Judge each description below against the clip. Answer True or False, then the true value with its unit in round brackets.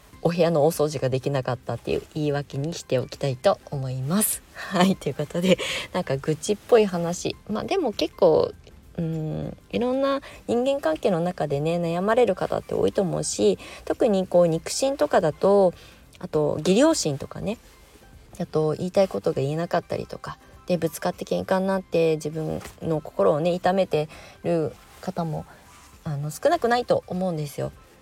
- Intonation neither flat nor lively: True (4.1 semitones)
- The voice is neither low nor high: True (170 Hz)